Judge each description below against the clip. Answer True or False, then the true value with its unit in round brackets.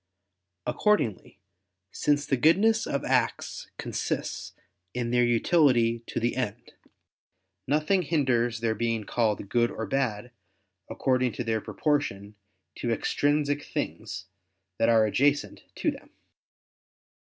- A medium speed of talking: False (115 wpm)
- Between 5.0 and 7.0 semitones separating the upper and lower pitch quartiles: False (4.1 semitones)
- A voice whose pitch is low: True (125 Hz)